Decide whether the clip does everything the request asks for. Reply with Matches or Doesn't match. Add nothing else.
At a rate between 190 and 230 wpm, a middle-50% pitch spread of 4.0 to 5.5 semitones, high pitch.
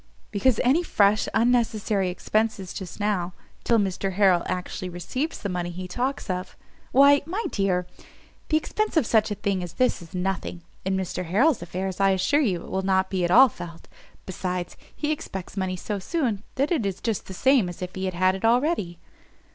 Matches